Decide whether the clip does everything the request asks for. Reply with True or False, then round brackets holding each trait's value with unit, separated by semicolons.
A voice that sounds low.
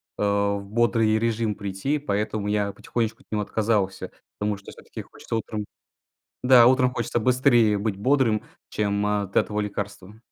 True (105 Hz)